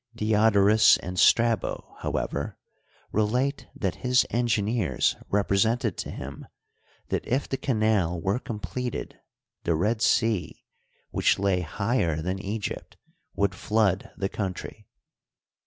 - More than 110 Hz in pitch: No, low, 105 Hz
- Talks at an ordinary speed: No, slow, 110 wpm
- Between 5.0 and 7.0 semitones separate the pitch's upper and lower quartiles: No, average, 3.2 semitones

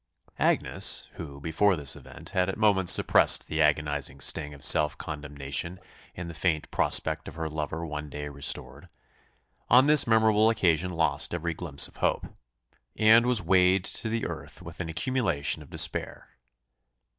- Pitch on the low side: Yes, very low, 85 Hz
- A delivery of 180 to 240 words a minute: No, average, 155 wpm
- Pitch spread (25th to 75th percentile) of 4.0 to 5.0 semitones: Yes, average, 4.6 semitones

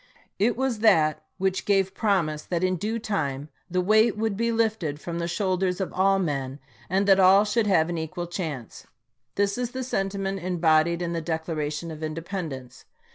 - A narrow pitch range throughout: No, average, 4.0 semitones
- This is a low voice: No, medium, 185 Hz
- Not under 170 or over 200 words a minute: Yes, average, 180 wpm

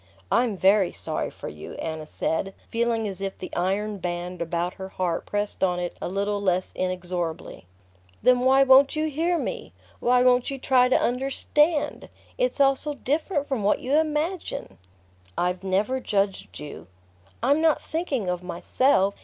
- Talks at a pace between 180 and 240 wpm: No, average, 160 wpm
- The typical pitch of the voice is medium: No, high, 210 Hz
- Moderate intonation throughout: No, wide, 6.9 semitones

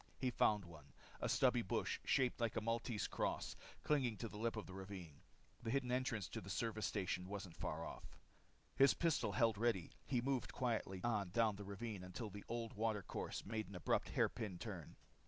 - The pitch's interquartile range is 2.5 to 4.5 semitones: Yes, average, 3.6 semitones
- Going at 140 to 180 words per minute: No, average, 190 wpm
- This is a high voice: No, low, 110 Hz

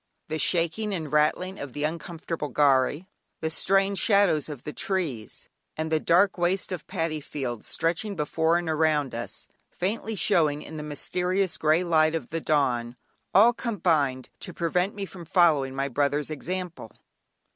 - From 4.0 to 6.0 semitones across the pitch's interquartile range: No, average, 3.6 semitones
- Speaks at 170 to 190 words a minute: No, average, 155 wpm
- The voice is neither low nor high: Yes, medium, 160 Hz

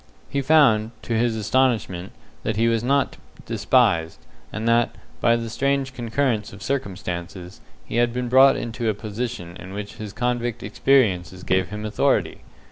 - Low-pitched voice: Yes, low, 115 Hz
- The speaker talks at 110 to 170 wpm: Yes, average, 155 wpm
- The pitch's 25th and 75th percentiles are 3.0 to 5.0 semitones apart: Yes, average, 3.6 semitones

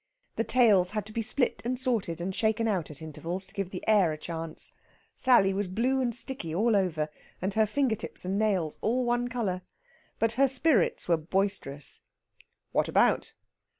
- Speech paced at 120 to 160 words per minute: No, average, 185 wpm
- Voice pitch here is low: No, high, 205 Hz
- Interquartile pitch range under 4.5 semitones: No, average, 5.0 semitones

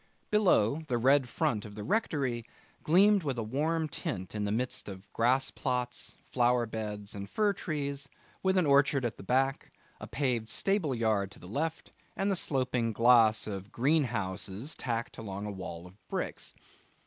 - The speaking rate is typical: Yes, average, 170 wpm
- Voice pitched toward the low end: Yes, low, 125 Hz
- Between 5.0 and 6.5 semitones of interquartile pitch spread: Yes, average, 5.3 semitones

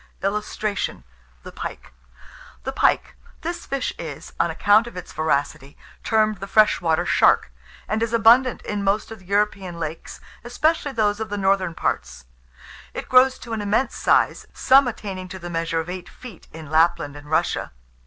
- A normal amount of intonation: Yes, average, 5.0 semitones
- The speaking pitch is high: Yes, high, 200 Hz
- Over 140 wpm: Yes, average, 165 wpm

